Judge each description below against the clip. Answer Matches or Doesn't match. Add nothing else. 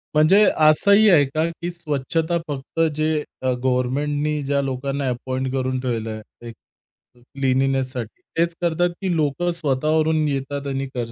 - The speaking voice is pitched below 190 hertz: Matches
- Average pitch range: Matches